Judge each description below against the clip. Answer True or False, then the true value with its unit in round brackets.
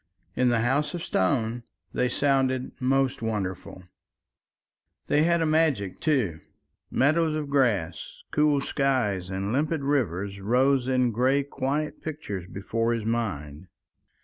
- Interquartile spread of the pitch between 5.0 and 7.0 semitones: True (5.6 semitones)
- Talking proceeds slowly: True (125 wpm)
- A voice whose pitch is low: True (125 Hz)